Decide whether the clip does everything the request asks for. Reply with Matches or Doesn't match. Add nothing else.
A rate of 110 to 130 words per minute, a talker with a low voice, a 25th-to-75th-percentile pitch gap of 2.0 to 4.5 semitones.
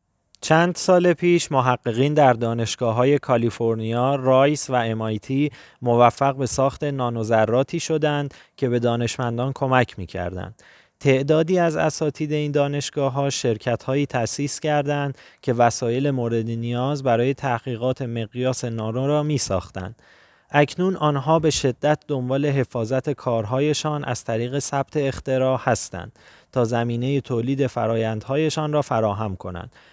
Matches